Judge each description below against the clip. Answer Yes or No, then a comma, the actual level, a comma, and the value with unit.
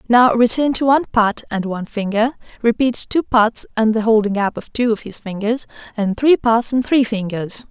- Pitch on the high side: Yes, high, 225 Hz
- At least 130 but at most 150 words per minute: No, average, 200 wpm